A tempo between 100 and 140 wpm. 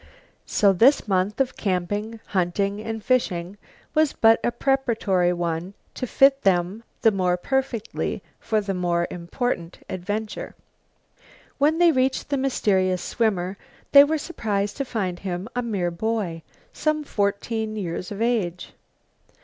Yes: slow, 135 wpm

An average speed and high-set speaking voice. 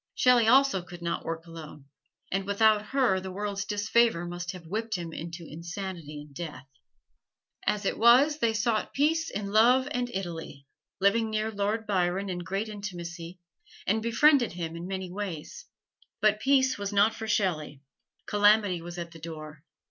Yes: average, 165 wpm; high, 200 Hz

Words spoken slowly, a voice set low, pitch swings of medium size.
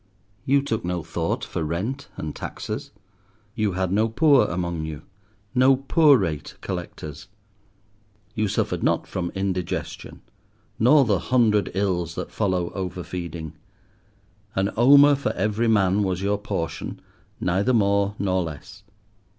Yes: slow, 130 wpm; low, 100 Hz; average, 4.1 semitones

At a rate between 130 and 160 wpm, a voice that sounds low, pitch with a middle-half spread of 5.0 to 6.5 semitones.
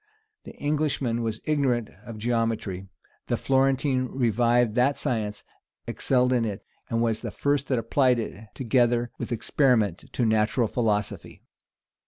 No: slow, 135 wpm; low, 120 Hz; average, 2.8 semitones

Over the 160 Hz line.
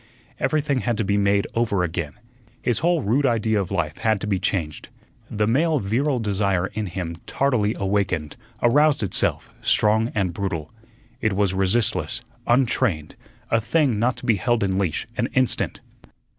No: low, 105 Hz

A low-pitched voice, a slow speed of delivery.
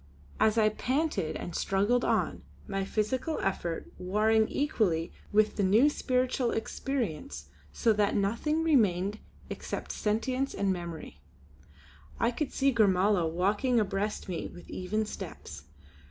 No: high, 210 Hz; slow, 125 wpm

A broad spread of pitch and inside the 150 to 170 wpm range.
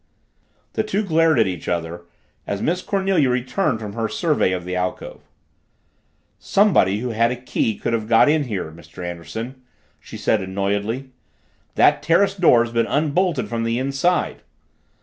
Yes: wide, 7.5 semitones; average, 155 wpm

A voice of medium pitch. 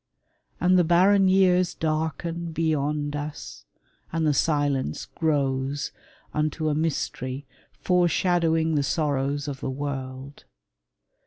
Yes: medium, 155 Hz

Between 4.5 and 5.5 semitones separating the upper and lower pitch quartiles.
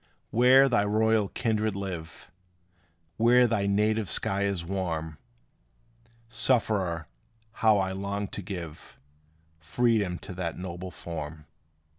No: average, 4.0 semitones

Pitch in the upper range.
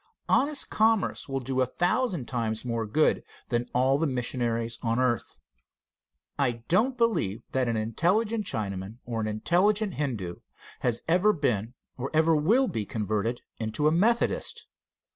No: low, 130 Hz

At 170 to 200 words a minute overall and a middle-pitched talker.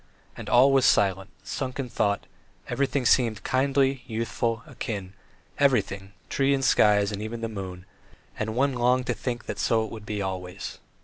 No: average, 175 wpm; low, 115 Hz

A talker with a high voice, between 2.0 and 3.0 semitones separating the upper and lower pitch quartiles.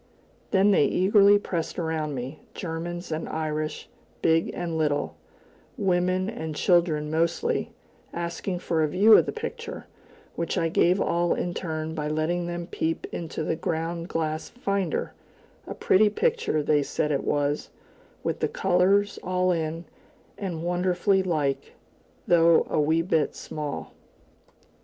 No: medium, 170 Hz; average, 2.7 semitones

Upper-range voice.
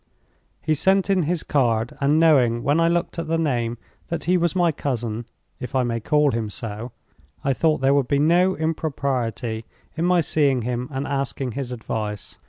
No: medium, 140 Hz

